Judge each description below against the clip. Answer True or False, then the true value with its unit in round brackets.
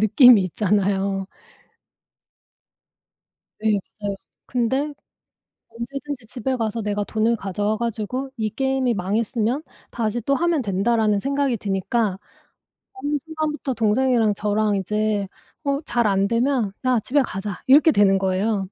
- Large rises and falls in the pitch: False (4.3 semitones)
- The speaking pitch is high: True (225 Hz)